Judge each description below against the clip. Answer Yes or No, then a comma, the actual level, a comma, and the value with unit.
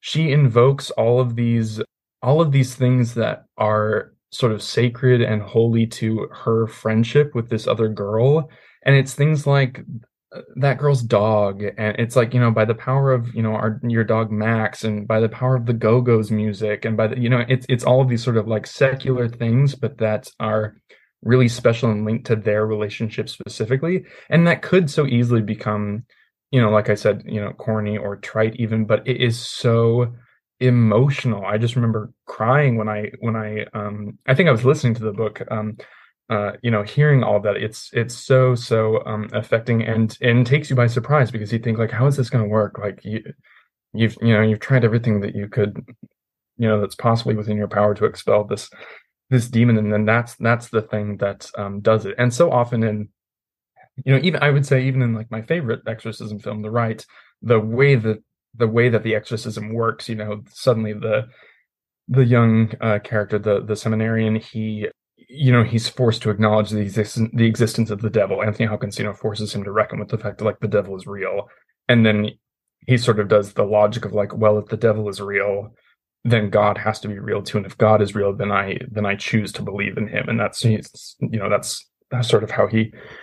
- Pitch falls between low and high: No, low, 115 Hz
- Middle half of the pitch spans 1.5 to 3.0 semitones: Yes, narrow, 2.5 semitones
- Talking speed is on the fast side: Yes, fast, 215 wpm